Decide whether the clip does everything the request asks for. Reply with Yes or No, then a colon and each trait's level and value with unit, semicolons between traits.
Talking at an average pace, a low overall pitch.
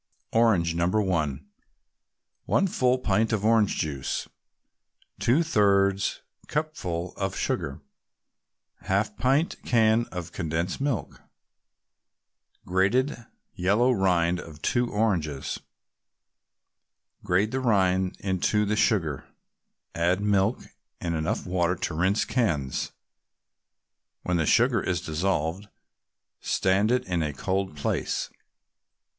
No: slow, 100 wpm; very low, 95 Hz